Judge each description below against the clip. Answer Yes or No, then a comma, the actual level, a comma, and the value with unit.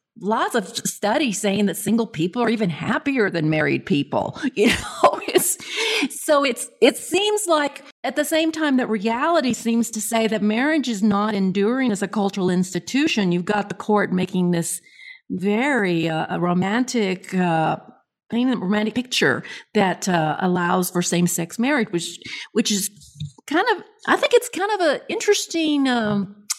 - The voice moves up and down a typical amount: No, wide, 7.5 semitones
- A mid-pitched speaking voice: No, high, 220 Hz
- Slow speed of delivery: No, average, 160 wpm